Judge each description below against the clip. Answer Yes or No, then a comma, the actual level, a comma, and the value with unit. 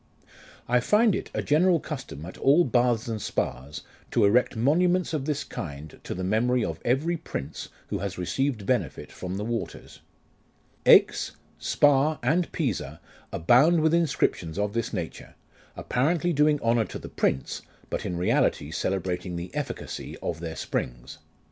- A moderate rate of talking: Yes, average, 155 wpm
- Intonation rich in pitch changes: Yes, wide, 8.6 semitones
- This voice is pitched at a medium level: No, low, 120 Hz